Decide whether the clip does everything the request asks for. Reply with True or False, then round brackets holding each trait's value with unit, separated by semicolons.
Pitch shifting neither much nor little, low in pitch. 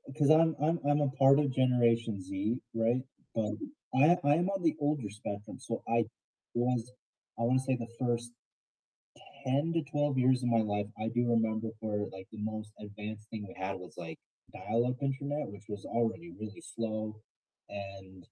True (4.1 semitones; 115 Hz)